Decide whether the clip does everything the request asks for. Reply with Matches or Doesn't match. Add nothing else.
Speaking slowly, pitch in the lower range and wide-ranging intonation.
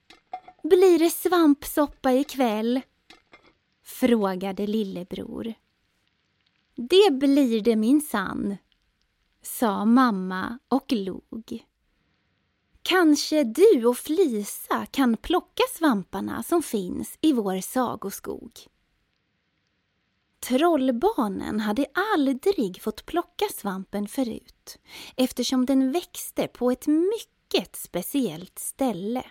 Doesn't match